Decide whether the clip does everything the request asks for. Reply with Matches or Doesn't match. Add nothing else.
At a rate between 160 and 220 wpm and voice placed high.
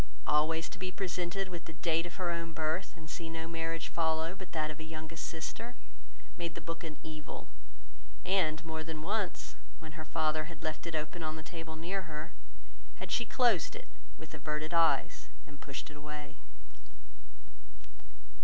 Doesn't match